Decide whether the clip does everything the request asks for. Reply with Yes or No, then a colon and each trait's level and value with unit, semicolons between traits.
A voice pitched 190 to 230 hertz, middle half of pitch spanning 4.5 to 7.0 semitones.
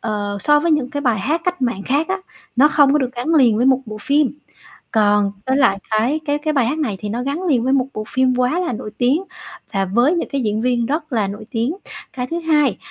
No: very high, 255 Hz; average, 5.2 semitones